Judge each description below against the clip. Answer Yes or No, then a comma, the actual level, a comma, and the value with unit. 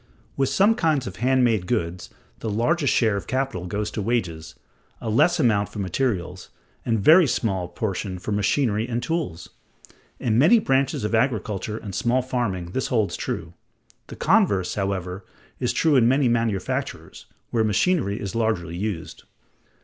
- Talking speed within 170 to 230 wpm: No, average, 160 wpm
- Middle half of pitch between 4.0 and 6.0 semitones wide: Yes, average, 5.1 semitones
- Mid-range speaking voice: No, low, 110 Hz